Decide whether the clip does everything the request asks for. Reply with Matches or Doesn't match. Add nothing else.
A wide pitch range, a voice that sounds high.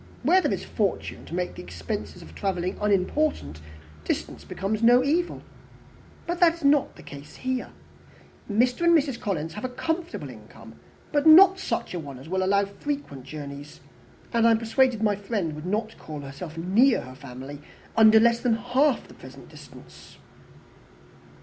Matches